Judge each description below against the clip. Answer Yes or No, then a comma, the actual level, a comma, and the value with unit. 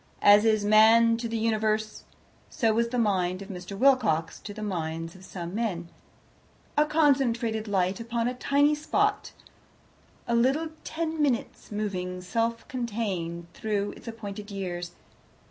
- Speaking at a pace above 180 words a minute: No, average, 145 wpm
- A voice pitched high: Yes, high, 220 Hz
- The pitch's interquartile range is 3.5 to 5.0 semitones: Yes, average, 3.8 semitones